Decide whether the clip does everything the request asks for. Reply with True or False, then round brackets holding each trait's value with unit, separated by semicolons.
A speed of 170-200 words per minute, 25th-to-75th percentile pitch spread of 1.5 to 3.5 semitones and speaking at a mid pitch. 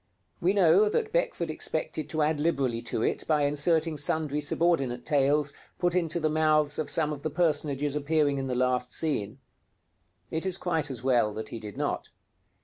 True (180 wpm; 3.0 semitones; 150 Hz)